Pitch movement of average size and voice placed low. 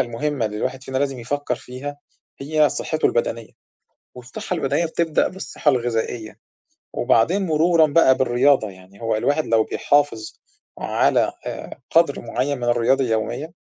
Yes: average, 4.0 semitones; low, 130 Hz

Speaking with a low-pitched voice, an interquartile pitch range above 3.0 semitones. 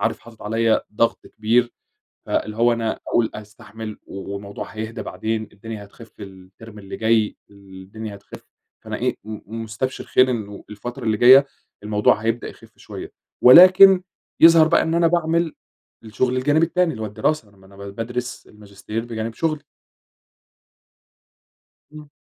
Yes: low, 115 Hz; average, 3.4 semitones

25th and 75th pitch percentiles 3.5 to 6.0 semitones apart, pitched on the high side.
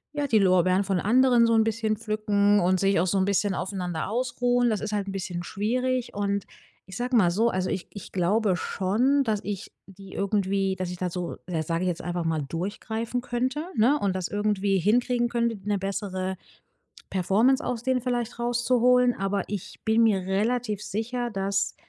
Yes: average, 3.9 semitones; high, 205 Hz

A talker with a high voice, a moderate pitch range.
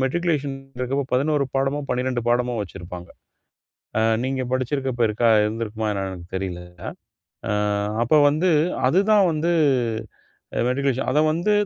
No: low, 130 Hz; average, 4.3 semitones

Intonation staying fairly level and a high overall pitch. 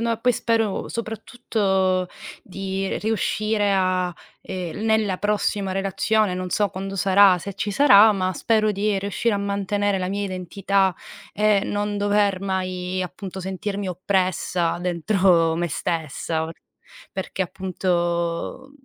Yes: narrow, 2.1 semitones; high, 195 Hz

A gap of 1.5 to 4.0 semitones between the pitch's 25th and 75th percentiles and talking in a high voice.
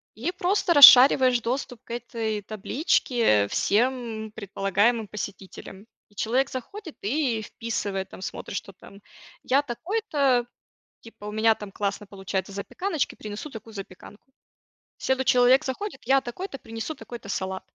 No: average, 4.4 semitones; high, 230 Hz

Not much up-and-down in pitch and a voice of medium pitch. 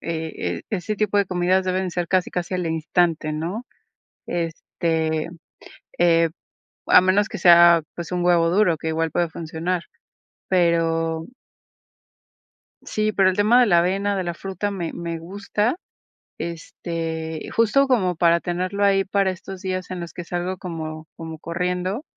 Yes: narrow, 2.3 semitones; medium, 175 Hz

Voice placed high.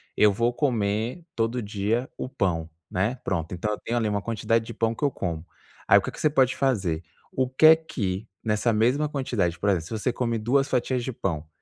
No: low, 115 Hz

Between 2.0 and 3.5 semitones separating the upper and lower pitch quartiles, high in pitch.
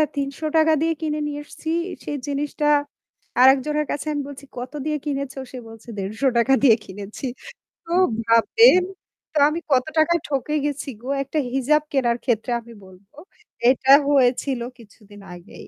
No: average, 4.1 semitones; very high, 275 Hz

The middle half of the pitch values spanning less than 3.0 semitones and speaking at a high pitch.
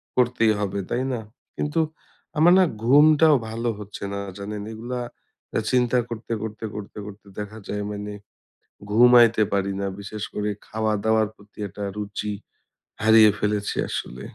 No: narrow, 2.6 semitones; low, 110 Hz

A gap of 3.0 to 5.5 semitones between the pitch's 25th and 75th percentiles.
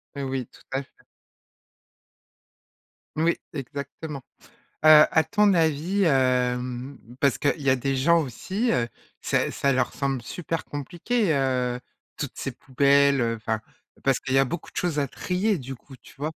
Yes: average, 3.7 semitones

